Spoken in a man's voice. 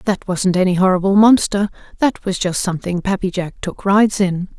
No: female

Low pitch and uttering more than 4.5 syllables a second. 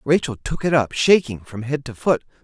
Yes: low, 130 Hz; 5.1 syllables/s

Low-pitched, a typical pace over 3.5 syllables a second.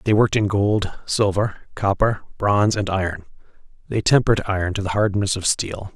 Yes: low, 100 Hz; 5.5 syllables/s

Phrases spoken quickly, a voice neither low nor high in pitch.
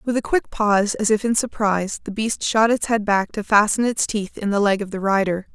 No: fast, 260 wpm; high, 210 Hz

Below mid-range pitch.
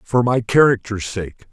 Yes: low, 110 Hz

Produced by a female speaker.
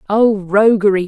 Yes: female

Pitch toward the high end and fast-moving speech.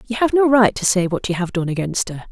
Yes: high, 205 Hz; fast, 310 wpm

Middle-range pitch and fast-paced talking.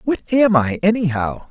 No: medium, 180 Hz; average, 160 wpm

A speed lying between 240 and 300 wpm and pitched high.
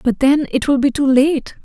Yes: fast, 255 wpm; very high, 275 Hz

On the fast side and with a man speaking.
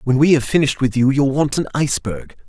Yes: fast, 240 wpm; male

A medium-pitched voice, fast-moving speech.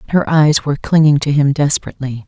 No: medium, 145 Hz; average, 185 wpm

